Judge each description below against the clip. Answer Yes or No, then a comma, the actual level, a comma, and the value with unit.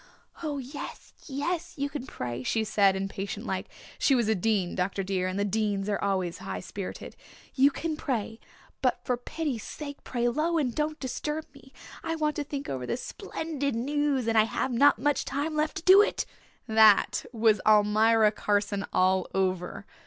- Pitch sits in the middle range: No, high, 235 Hz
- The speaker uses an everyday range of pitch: No, wide, 6.2 semitones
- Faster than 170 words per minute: Yes, average, 180 wpm